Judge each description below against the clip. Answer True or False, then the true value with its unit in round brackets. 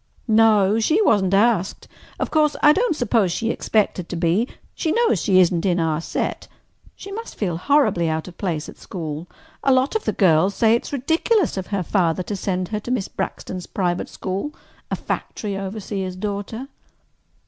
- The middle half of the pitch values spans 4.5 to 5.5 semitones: True (5.2 semitones)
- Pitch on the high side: True (200 Hz)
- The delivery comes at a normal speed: True (180 wpm)